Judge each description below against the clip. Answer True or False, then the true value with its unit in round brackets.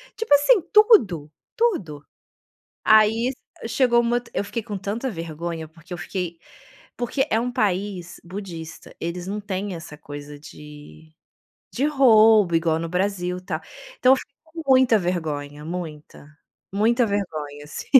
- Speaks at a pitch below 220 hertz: True (190 Hz)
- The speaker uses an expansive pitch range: True (6.4 semitones)